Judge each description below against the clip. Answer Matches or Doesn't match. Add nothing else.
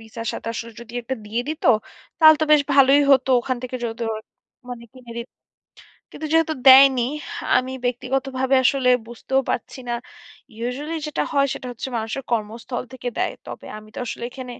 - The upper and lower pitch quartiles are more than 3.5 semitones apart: Doesn't match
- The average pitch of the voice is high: Matches